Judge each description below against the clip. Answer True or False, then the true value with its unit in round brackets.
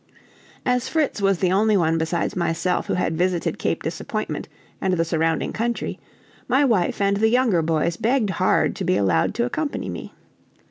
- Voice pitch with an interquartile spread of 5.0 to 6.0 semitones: True (5.6 semitones)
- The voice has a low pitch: False (185 Hz)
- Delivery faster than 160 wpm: True (175 wpm)